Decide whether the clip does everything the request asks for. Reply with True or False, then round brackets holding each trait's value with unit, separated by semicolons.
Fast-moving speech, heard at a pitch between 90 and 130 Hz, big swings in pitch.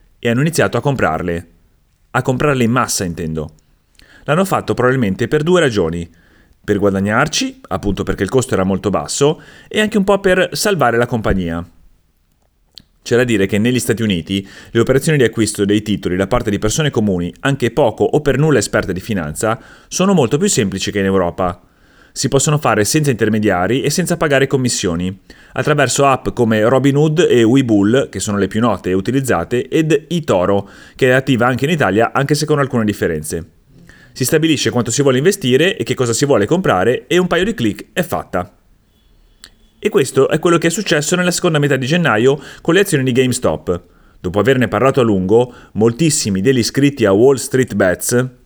True (185 wpm; 120 Hz; 6.0 semitones)